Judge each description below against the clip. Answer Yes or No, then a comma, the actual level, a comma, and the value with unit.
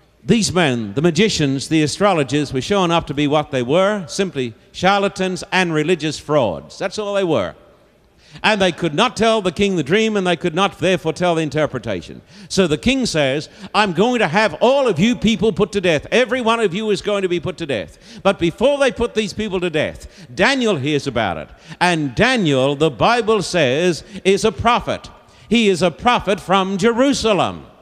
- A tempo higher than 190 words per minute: Yes, average, 200 wpm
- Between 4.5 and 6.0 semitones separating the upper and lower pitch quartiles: Yes, average, 4.9 semitones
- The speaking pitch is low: No, high, 190 Hz